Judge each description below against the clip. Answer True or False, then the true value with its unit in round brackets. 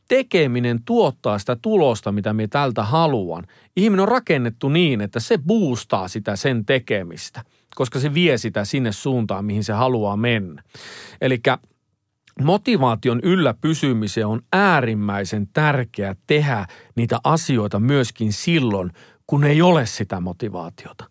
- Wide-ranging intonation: True (6.3 semitones)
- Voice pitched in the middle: False (120 Hz)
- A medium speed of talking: True (130 wpm)